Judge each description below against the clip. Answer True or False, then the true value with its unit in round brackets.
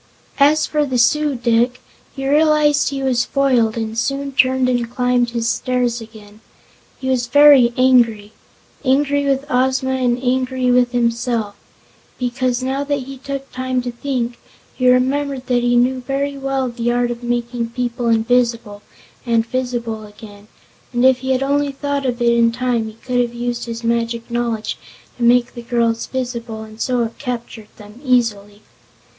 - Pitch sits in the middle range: False (245 Hz)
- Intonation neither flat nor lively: False (2.0 semitones)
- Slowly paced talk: False (165 wpm)